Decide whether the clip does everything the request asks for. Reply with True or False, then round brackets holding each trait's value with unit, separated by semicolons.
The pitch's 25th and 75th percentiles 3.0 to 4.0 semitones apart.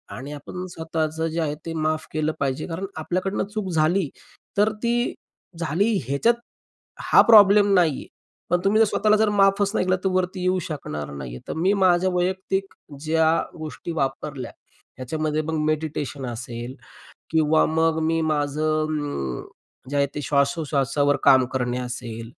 False (4.6 semitones)